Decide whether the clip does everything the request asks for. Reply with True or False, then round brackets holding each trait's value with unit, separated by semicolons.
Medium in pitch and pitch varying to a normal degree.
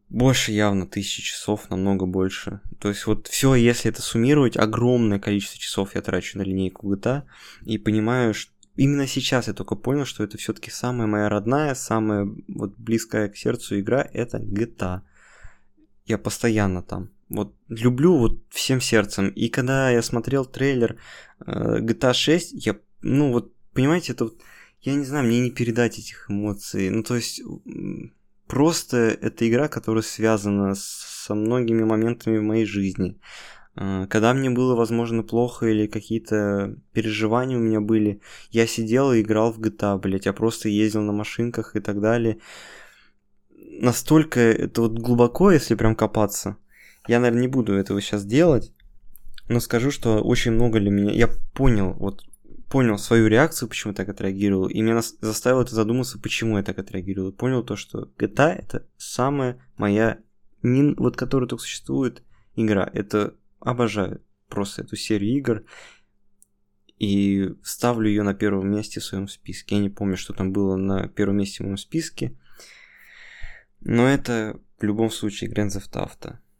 False (110 Hz; 3.1 semitones)